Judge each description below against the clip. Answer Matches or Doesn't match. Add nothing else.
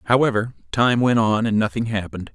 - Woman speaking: Doesn't match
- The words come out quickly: Doesn't match